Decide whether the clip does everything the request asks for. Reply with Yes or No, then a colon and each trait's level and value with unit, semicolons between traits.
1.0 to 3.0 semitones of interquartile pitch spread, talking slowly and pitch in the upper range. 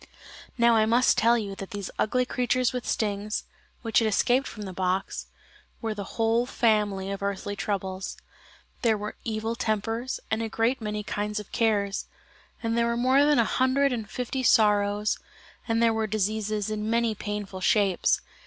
No: narrow, 2.4 semitones; average, 170 wpm; high, 220 Hz